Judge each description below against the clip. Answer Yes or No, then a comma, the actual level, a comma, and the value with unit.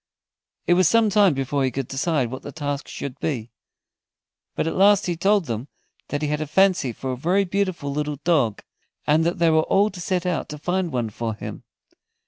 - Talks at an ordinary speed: No, fast, 210 wpm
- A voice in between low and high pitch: Yes, medium, 155 Hz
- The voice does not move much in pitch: No, average, 5.3 semitones